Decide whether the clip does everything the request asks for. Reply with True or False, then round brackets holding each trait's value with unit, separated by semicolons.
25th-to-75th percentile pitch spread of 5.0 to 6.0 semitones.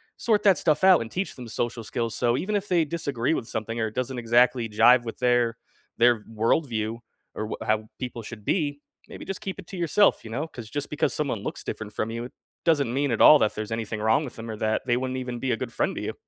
False (4.4 semitones)